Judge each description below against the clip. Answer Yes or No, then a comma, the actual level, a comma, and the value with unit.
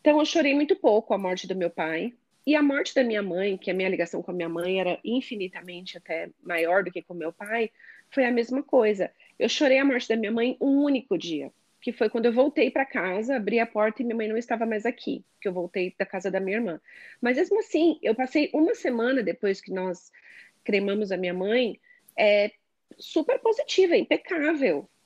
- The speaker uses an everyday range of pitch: No, wide, 6.4 semitones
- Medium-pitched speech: No, high, 225 Hz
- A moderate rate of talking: No, fast, 220 wpm